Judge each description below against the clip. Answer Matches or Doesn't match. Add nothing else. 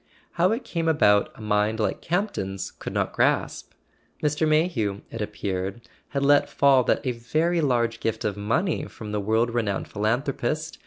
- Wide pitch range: Matches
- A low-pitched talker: Matches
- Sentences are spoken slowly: Doesn't match